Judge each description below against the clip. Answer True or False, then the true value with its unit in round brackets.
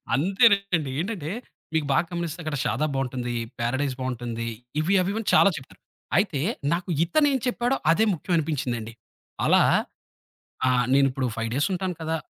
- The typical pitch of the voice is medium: True (155 Hz)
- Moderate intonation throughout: False (6.4 semitones)